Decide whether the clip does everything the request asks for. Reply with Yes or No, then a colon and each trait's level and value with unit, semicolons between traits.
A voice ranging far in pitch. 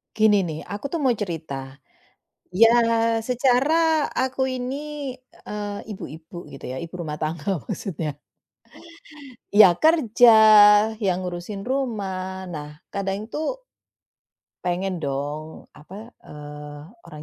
Yes: wide, 6.0 semitones